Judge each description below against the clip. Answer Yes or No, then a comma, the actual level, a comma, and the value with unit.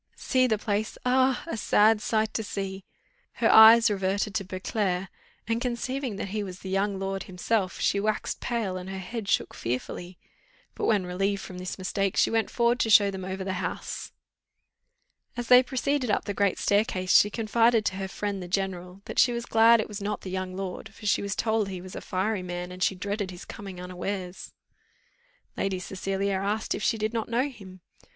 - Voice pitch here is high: Yes, high, 200 Hz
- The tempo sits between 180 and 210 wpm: Yes, average, 200 wpm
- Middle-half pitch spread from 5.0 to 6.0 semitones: No, average, 2.8 semitones